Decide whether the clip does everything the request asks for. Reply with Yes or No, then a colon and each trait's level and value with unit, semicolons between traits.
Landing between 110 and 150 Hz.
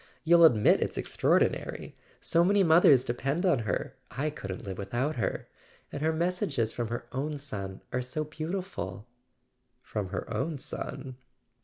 Yes: medium, 140 Hz